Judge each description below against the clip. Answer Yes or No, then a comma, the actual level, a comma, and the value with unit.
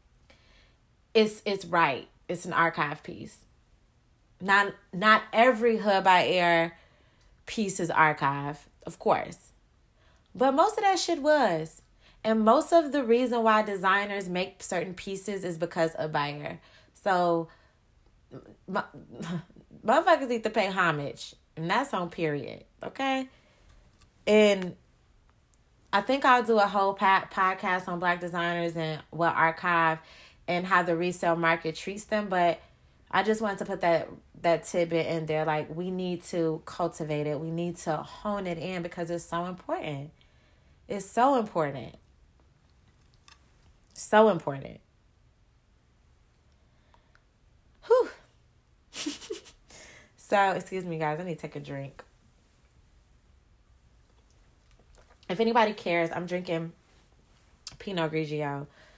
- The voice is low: No, medium, 175 Hz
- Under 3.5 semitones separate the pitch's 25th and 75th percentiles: No, average, 4.2 semitones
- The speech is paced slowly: Yes, slow, 125 wpm